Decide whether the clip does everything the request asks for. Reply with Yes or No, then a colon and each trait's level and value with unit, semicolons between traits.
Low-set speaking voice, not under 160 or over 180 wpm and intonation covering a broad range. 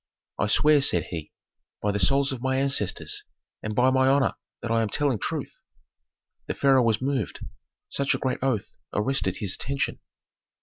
No: low, 130 Hz; average, 170 wpm; average, 4.5 semitones